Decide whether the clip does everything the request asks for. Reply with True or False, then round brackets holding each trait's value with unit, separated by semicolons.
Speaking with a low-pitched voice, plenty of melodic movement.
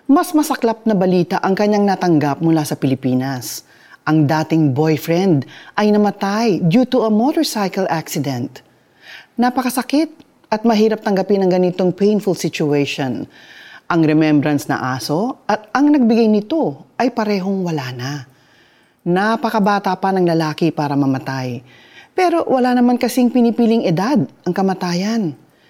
False (190 Hz; 6.8 semitones)